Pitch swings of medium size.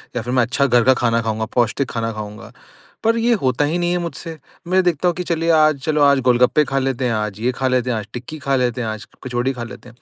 Yes: average, 4.5 semitones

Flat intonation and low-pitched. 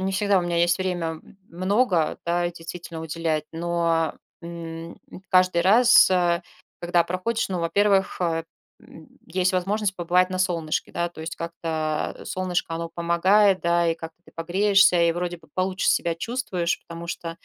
No: narrow, 1.9 semitones; medium, 175 Hz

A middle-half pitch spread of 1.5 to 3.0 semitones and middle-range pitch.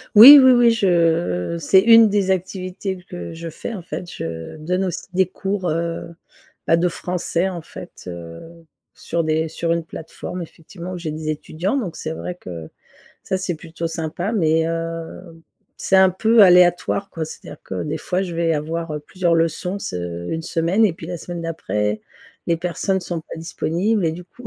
Yes: narrow, 2.6 semitones; medium, 170 Hz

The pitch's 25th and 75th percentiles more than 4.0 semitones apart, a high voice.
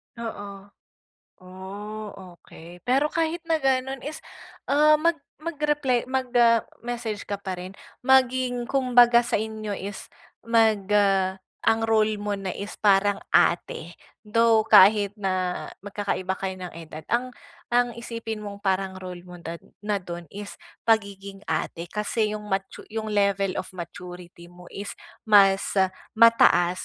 No: average, 3.7 semitones; high, 205 Hz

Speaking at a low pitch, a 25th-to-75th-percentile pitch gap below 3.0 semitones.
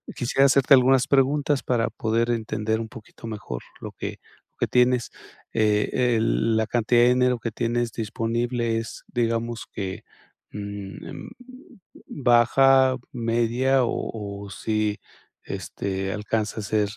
Yes: low, 115 Hz; narrow, 2.5 semitones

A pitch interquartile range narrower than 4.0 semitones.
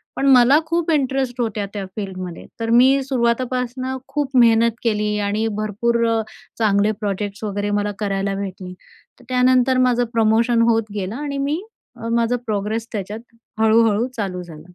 Yes: average, 3.5 semitones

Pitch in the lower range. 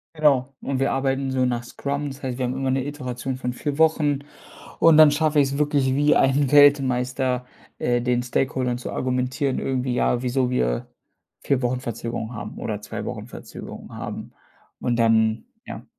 Yes: low, 130 Hz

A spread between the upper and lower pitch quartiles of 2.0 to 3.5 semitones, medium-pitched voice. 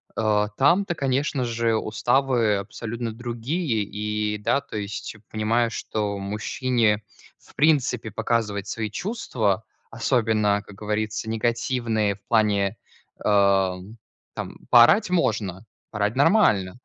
No: average, 2.7 semitones; low, 110 Hz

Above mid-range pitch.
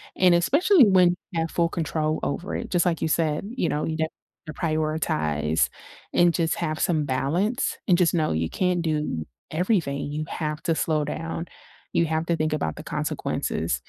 No: medium, 160 Hz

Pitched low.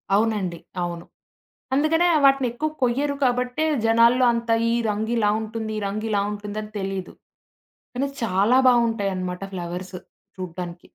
No: high, 220 Hz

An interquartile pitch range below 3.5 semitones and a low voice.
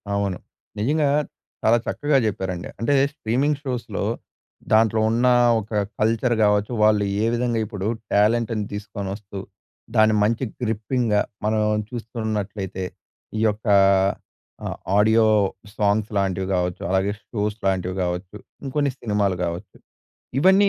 Yes: average, 2.7 semitones; low, 110 Hz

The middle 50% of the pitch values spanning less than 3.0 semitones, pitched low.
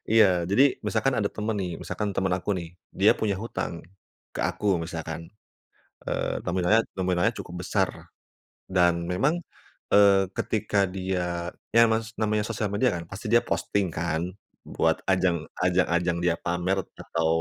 No: average, 3.4 semitones; very low, 95 Hz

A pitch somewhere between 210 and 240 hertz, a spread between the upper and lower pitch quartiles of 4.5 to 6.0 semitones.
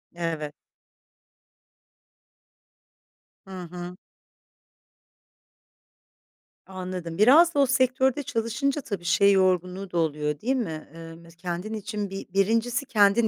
No: high, 195 Hz; wide, 5.5 semitones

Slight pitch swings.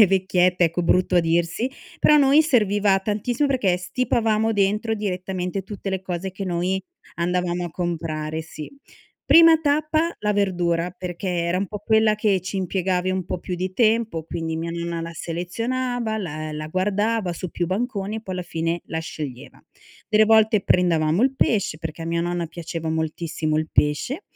No: average, 4.1 semitones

